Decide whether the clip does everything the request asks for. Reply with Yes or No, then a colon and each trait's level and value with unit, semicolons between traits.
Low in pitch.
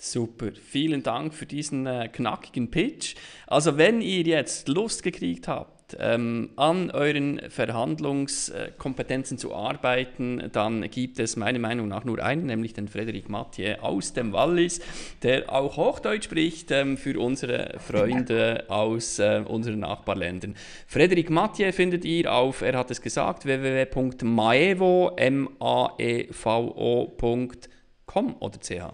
Yes: low, 125 Hz